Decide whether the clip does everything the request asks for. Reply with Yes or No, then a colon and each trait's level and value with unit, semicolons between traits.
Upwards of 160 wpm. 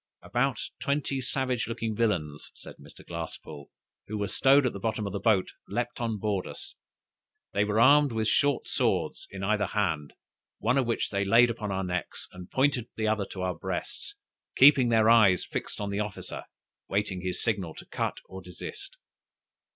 Yes: average, 180 wpm